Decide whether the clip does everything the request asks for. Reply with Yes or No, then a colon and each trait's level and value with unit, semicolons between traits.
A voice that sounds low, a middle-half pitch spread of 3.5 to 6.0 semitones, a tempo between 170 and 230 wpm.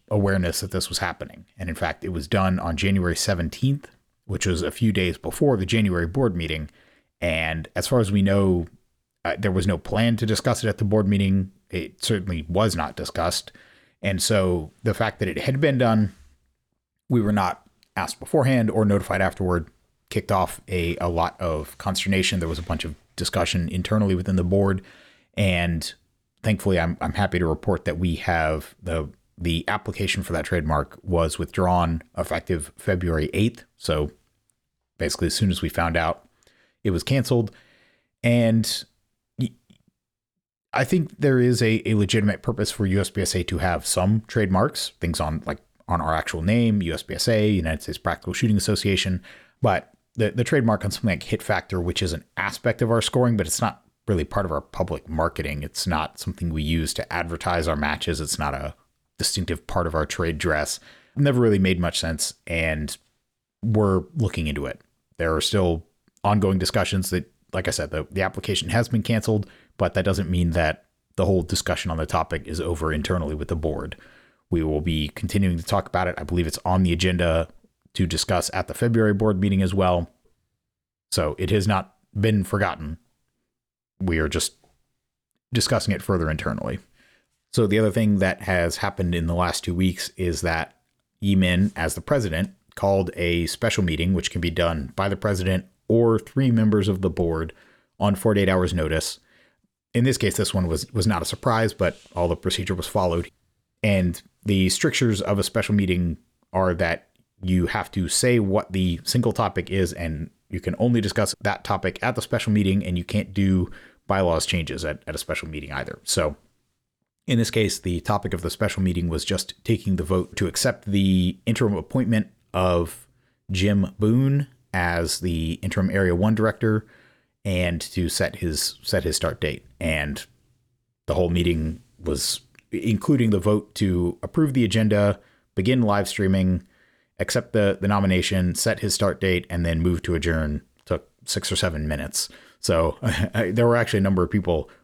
Yes: very low, 95 Hz; average, 3.9 semitones; average, 180 wpm